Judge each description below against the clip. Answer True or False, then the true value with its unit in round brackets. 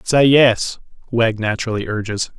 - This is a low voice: True (115 Hz)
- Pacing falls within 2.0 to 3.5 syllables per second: False (4.6 syllables/s)